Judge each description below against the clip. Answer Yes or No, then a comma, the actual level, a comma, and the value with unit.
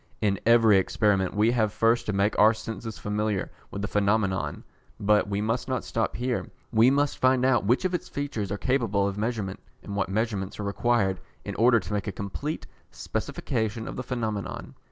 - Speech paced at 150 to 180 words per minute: No, average, 190 wpm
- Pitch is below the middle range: Yes, low, 110 Hz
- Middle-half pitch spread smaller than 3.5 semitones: Yes, average, 2.9 semitones